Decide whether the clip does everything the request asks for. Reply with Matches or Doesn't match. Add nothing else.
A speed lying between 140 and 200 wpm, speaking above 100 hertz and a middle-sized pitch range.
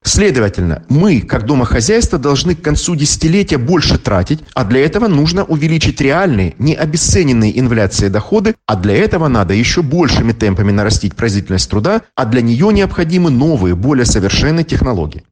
Doesn't match